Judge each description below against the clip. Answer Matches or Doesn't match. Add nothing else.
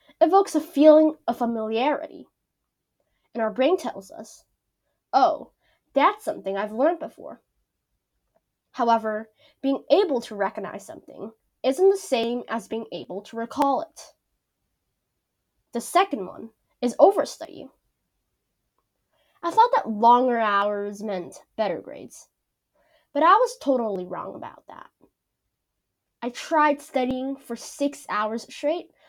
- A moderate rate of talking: Doesn't match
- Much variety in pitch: Matches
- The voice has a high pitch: Matches